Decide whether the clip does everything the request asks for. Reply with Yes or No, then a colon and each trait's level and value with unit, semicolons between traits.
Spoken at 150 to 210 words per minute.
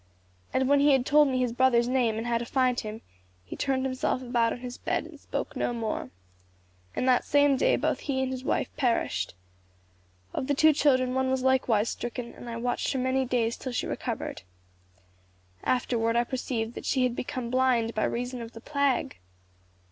Yes: average, 195 wpm